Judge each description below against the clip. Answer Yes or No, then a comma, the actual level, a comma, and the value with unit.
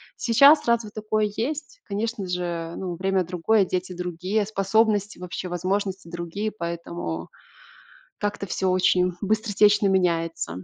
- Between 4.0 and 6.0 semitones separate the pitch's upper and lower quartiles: No, average, 3.3 semitones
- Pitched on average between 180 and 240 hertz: Yes, high, 190 Hz